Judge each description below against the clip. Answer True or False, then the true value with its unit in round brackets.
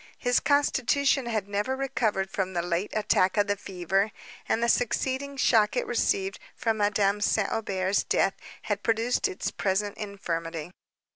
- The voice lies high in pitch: True (205 Hz)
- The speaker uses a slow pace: False (150 wpm)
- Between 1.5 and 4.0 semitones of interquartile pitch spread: True (3.5 semitones)